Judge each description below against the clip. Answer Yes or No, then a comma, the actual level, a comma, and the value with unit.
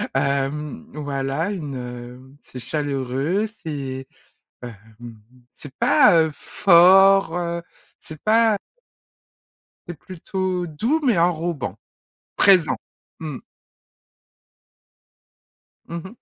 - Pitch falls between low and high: Yes, medium, 155 Hz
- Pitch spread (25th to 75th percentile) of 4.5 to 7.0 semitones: Yes, average, 5.3 semitones